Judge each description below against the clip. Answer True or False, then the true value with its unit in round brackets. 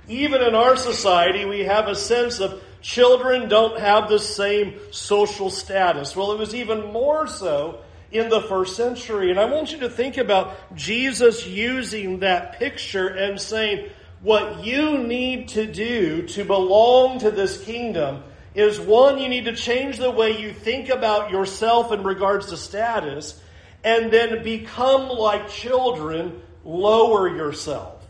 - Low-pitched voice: False (215 Hz)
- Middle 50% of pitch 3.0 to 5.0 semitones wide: True (3.8 semitones)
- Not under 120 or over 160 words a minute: True (155 wpm)